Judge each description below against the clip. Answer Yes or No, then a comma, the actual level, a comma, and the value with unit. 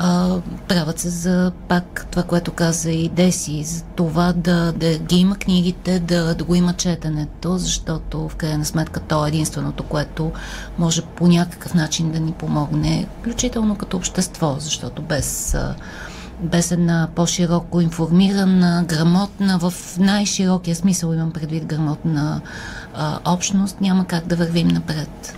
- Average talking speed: Yes, average, 140 wpm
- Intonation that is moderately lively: No, narrow, 2.0 semitones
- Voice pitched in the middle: Yes, medium, 170 Hz